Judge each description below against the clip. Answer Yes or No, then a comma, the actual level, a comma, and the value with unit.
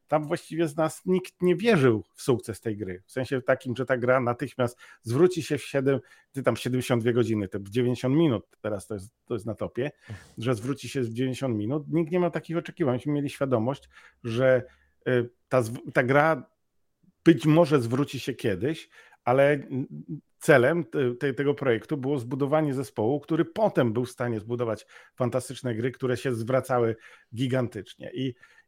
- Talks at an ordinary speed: No, fast, 165 wpm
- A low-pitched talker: Yes, low, 130 Hz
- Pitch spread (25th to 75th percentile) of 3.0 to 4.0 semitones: Yes, average, 3.3 semitones